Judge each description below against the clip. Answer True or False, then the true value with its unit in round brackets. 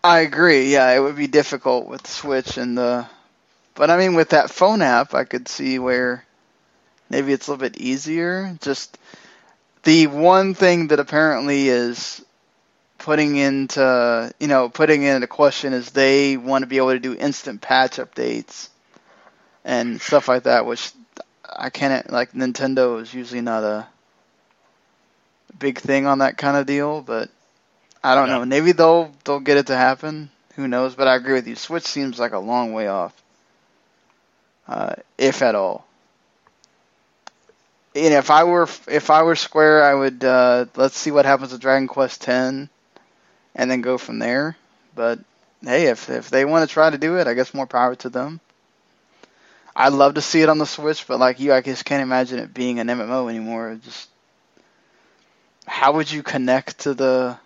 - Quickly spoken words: False (180 wpm)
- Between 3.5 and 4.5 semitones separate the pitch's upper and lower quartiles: False (2.9 semitones)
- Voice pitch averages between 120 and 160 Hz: True (135 Hz)